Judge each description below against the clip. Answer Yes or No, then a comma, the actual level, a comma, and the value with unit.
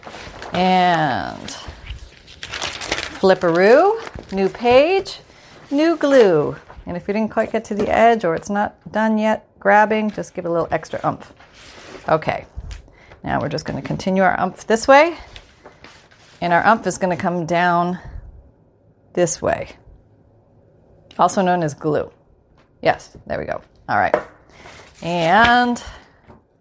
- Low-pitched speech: No, high, 195 Hz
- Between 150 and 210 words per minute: No, slow, 135 wpm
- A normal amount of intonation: Yes, average, 4.2 semitones